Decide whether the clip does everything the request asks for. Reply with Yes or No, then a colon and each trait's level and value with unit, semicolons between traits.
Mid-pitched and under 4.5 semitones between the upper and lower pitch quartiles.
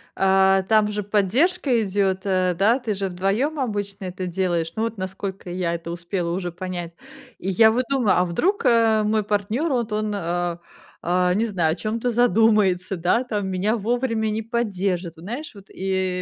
No: high, 200 Hz; average, 3.5 semitones